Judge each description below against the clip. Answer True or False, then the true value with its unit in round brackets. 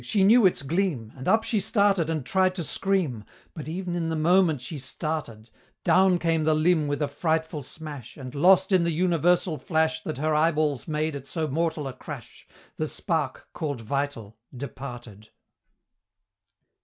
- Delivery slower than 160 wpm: False (170 wpm)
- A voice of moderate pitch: True (155 Hz)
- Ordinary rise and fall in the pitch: True (3.9 semitones)